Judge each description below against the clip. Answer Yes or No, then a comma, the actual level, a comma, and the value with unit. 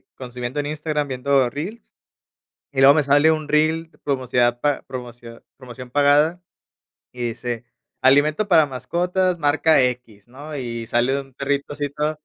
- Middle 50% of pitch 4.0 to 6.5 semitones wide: No, average, 3.4 semitones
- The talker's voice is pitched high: No, medium, 140 Hz